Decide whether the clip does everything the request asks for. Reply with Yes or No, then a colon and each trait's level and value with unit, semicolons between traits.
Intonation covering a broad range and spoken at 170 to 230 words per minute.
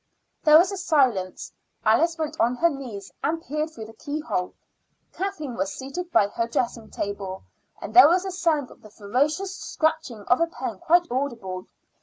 Yes: wide, 7.0 semitones; average, 175 wpm